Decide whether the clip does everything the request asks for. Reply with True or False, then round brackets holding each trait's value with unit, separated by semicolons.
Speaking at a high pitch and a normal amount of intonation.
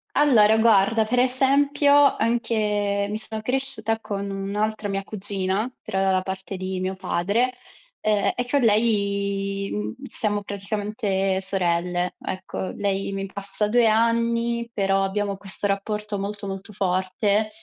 False (205 Hz; 2.3 semitones)